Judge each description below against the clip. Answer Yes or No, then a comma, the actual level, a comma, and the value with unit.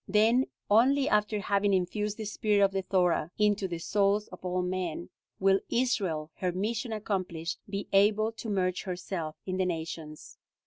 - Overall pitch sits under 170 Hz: No, high, 195 Hz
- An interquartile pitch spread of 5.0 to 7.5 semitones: No, average, 2.7 semitones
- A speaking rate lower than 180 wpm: Yes, average, 165 wpm